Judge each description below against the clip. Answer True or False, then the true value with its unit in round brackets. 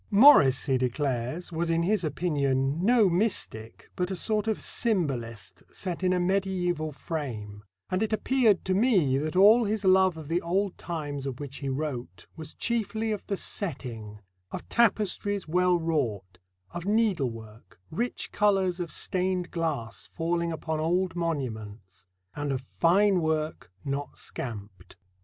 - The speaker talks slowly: False (145 wpm)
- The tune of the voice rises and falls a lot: True (6.1 semitones)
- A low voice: False (165 Hz)